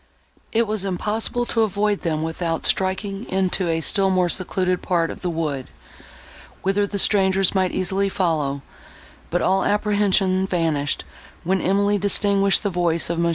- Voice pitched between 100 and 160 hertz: No, high, 190 Hz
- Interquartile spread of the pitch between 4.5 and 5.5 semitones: No, average, 2.8 semitones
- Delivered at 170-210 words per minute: No, average, 155 wpm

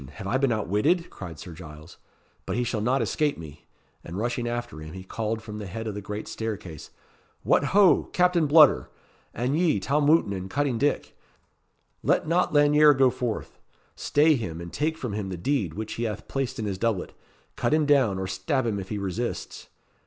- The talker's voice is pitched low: Yes, low, 115 Hz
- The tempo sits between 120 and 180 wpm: No, average, 195 wpm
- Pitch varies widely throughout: Yes, wide, 6.9 semitones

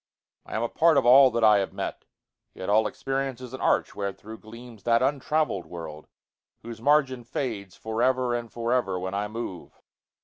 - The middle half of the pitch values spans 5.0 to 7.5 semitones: No, average, 3.8 semitones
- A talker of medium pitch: No, low, 115 Hz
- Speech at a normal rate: Yes, average, 170 wpm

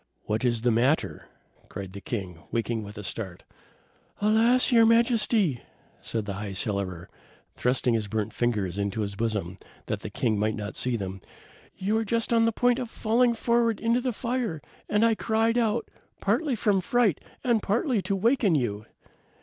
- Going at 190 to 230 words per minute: No, average, 175 wpm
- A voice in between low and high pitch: Yes, medium, 155 Hz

